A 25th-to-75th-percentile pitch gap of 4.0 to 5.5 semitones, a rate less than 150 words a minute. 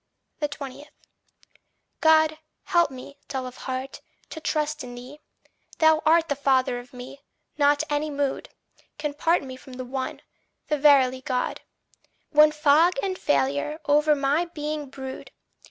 No: average, 2.8 semitones; average, 140 wpm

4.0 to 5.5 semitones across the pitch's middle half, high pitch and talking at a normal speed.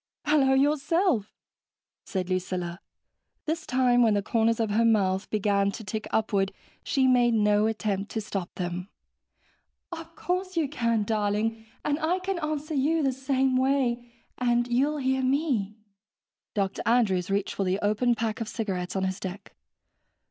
Yes: average, 4.9 semitones; high, 230 Hz; average, 155 wpm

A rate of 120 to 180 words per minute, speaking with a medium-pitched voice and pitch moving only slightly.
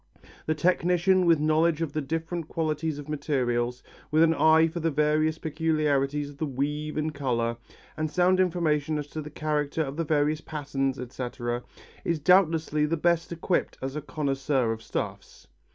Yes: average, 170 wpm; medium, 155 Hz; narrow, 2.3 semitones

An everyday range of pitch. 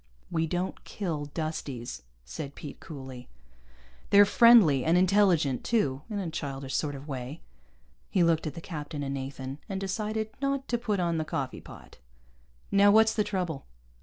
No: wide, 6.4 semitones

